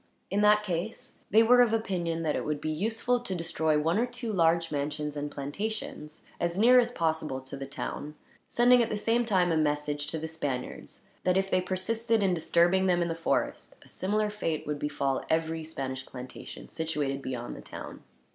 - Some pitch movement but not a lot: No, wide, 5.9 semitones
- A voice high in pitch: No, medium, 165 Hz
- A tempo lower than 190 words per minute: No, average, 195 wpm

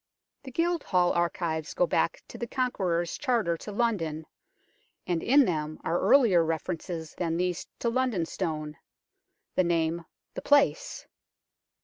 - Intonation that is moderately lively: No, wide, 6.5 semitones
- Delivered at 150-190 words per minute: No, slow, 135 wpm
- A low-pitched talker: No, medium, 175 Hz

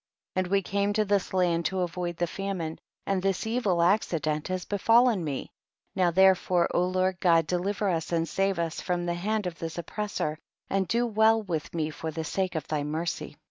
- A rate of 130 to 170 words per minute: No, fast, 205 wpm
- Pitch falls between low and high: Yes, medium, 180 Hz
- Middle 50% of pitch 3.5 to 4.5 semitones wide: No, average, 2.9 semitones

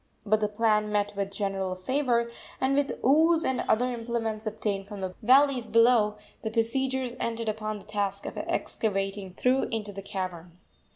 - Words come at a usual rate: Yes, average, 165 wpm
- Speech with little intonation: No, average, 3.4 semitones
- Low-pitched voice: No, high, 215 Hz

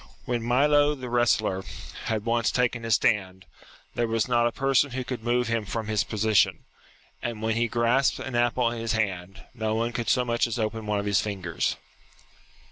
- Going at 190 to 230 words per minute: Yes, average, 195 wpm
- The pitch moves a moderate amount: No, narrow, 2.0 semitones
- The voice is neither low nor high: No, low, 115 Hz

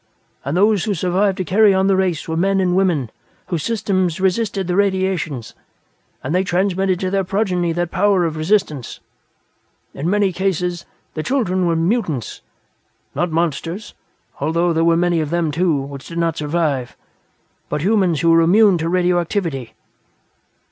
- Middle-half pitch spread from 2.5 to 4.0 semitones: Yes, average, 2.9 semitones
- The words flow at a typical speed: Yes, average, 160 wpm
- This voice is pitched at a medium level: Yes, medium, 175 Hz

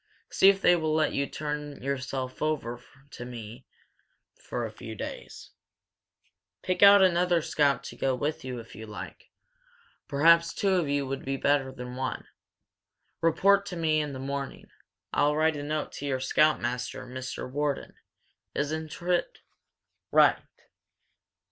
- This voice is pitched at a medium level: Yes, medium, 145 Hz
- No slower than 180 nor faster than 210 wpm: No, average, 150 wpm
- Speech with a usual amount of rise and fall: Yes, average, 3.5 semitones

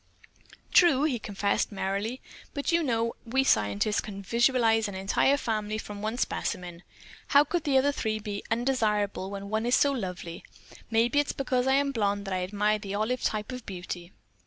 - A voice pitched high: Yes, high, 220 Hz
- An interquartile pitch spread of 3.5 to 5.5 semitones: Yes, average, 4.2 semitones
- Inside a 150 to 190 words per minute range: Yes, average, 185 wpm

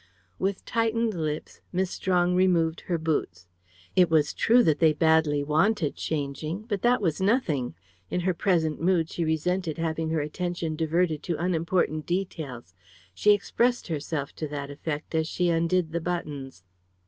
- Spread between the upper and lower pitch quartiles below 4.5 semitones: Yes, average, 3.0 semitones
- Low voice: No, medium, 165 Hz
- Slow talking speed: No, average, 155 wpm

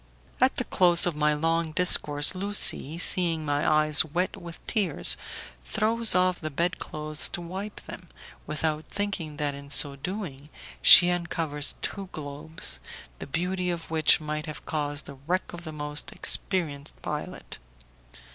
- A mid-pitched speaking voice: Yes, medium, 160 Hz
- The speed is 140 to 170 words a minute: Yes, average, 150 wpm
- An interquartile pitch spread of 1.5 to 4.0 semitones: Yes, average, 3.3 semitones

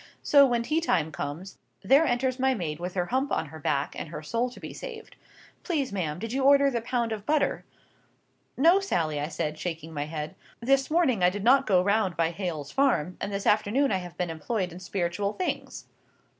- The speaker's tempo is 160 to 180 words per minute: No, fast, 205 wpm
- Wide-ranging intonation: Yes, wide, 8.0 semitones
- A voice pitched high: Yes, high, 200 Hz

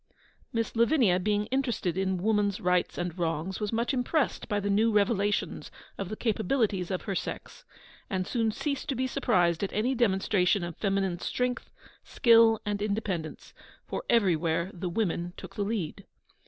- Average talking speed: Yes, average, 160 wpm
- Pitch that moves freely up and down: No, average, 4.0 semitones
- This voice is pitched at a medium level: No, high, 205 Hz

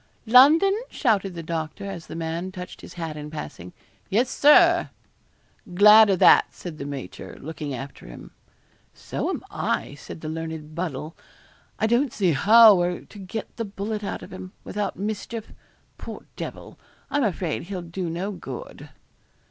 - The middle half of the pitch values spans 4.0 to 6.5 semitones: Yes, average, 5.2 semitones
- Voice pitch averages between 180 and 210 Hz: Yes, medium, 185 Hz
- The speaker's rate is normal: Yes, average, 160 wpm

